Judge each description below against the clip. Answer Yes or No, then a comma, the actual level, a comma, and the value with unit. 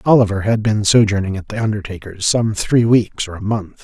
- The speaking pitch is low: Yes, low, 105 Hz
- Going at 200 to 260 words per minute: Yes, fast, 205 wpm